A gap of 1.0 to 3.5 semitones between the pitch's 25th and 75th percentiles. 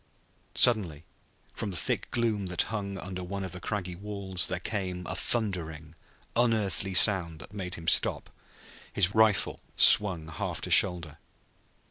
Yes: average, 2.9 semitones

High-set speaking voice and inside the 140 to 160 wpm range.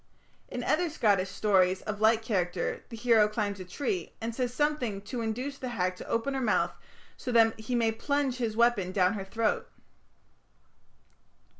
No: high, 225 Hz; average, 170 wpm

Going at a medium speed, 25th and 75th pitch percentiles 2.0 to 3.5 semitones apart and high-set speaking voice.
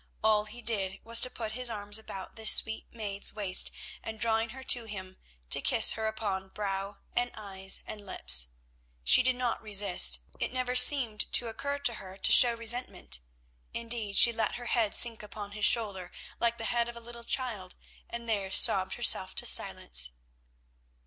Yes: average, 180 wpm; average, 3.0 semitones; high, 220 Hz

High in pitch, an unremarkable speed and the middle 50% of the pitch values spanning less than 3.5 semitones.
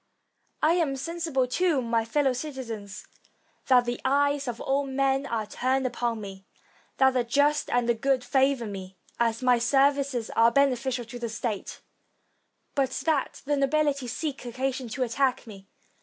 Yes: very high, 260 Hz; average, 155 wpm; average, 2.9 semitones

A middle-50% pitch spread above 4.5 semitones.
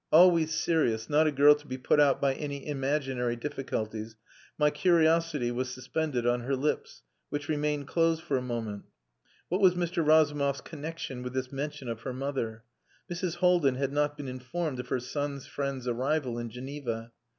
No: average, 3.4 semitones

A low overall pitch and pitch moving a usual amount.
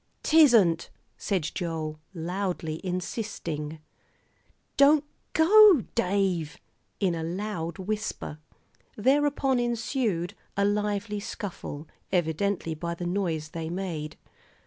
No: high, 190 Hz; average, 4.6 semitones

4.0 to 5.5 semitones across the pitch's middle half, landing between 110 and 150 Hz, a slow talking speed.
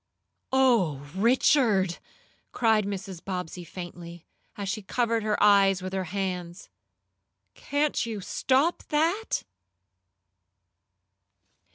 No: average, 4.7 semitones; high, 200 Hz; slow, 90 wpm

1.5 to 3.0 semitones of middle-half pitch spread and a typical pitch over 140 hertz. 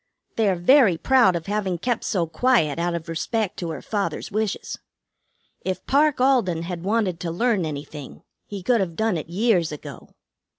No: average, 5.1 semitones; medium, 185 Hz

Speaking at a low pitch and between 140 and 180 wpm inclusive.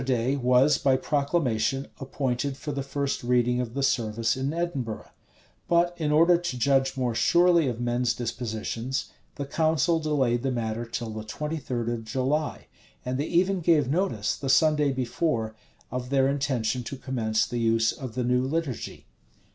Yes: low, 130 Hz; average, 170 wpm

